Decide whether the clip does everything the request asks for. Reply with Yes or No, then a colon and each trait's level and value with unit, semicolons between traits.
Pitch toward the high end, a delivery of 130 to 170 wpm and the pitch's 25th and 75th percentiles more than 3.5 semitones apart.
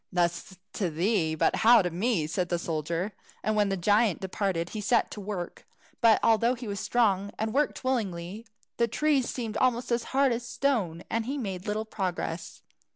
No: high, 210 Hz; average, 190 wpm; average, 4.8 semitones